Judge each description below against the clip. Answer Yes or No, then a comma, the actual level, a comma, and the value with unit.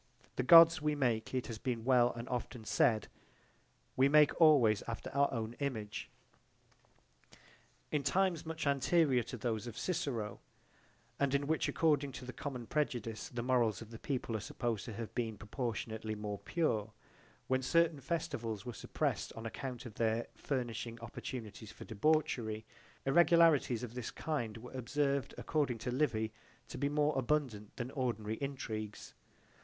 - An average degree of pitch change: Yes, average, 4.3 semitones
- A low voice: Yes, low, 125 Hz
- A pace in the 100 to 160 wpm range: Yes, average, 155 wpm